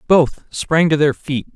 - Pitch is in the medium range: Yes, medium, 150 Hz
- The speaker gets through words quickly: No, average, 190 wpm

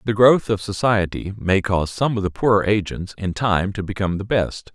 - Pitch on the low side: Yes, low, 100 Hz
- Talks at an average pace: No, fast, 215 wpm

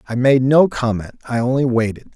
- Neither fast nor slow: Yes, average, 195 wpm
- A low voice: Yes, low, 125 Hz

